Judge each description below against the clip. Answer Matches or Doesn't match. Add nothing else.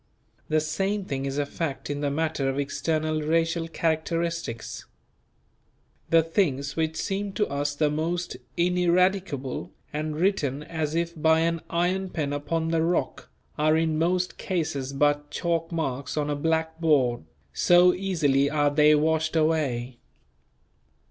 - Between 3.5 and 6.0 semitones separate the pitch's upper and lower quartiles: Doesn't match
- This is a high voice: Doesn't match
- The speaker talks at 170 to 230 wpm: Doesn't match